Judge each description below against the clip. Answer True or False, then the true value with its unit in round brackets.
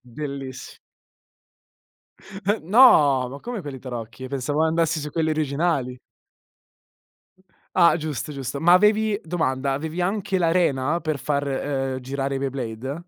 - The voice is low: False (145 Hz)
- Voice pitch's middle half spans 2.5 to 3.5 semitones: False (4.1 semitones)